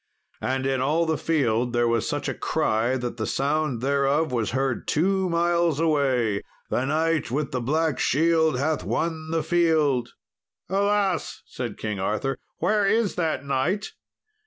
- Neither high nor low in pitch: Yes, medium, 145 Hz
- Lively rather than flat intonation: No, average, 4.7 semitones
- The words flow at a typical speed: Yes, average, 155 wpm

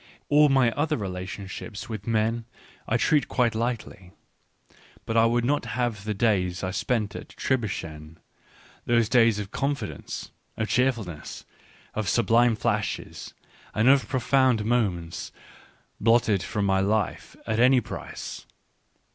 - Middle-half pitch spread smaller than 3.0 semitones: No, average, 3.3 semitones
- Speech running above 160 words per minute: No, average, 140 wpm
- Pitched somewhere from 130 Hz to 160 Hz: No, low, 115 Hz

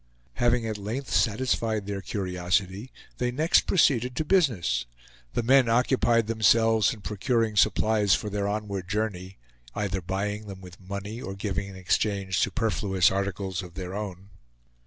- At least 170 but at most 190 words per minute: No, average, 145 wpm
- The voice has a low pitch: Yes, low, 105 Hz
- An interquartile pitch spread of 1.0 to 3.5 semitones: Yes, average, 3.0 semitones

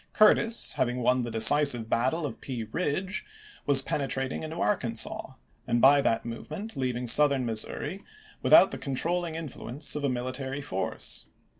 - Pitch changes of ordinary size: Yes, average, 3.8 semitones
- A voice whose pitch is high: No, low, 135 Hz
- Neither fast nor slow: Yes, average, 155 wpm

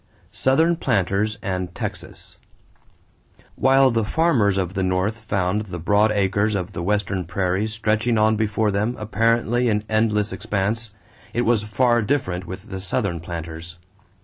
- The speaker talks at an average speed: Yes, average, 145 wpm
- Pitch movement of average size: Yes, average, 3.1 semitones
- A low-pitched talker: Yes, low, 105 Hz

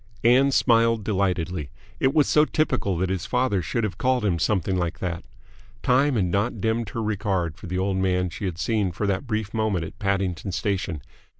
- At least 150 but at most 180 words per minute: No, average, 195 wpm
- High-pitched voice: No, low, 100 Hz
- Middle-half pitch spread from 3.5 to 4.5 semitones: Yes, average, 3.8 semitones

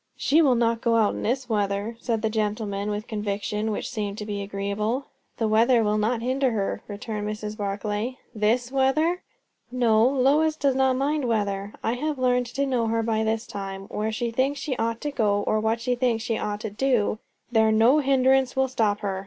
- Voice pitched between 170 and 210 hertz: No, high, 225 Hz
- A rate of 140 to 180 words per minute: No, average, 200 wpm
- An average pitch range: Yes, average, 3.5 semitones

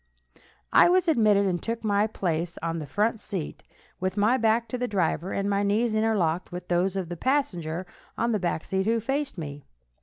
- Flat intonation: No, average, 4.4 semitones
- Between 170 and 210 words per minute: Yes, average, 200 wpm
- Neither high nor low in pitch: No, high, 200 Hz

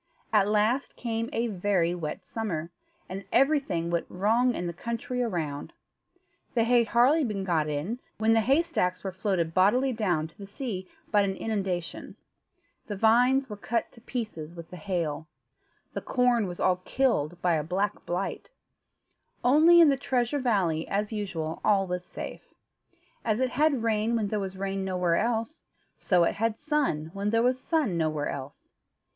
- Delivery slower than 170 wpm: No, average, 175 wpm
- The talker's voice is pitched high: Yes, high, 205 Hz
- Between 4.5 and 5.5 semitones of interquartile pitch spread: Yes, average, 5.2 semitones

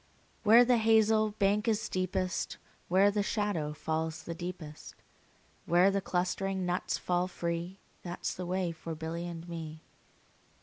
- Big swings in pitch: No, average, 3.3 semitones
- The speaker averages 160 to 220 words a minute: No, average, 150 wpm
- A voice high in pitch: No, medium, 180 Hz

